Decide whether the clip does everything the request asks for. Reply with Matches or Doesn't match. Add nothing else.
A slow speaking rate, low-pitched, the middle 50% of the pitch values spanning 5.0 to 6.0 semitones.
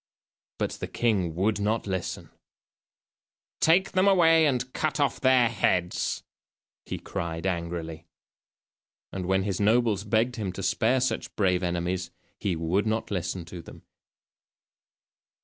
Matches